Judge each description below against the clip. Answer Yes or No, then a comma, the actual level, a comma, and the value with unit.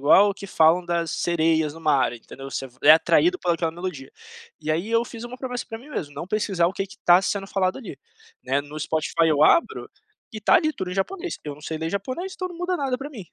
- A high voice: No, medium, 180 Hz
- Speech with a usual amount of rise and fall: No, wide, 6.6 semitones